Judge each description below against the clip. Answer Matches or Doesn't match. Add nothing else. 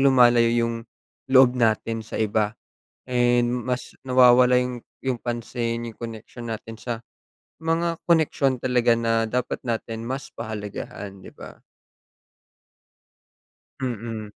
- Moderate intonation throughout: Doesn't match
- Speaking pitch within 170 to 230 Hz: Doesn't match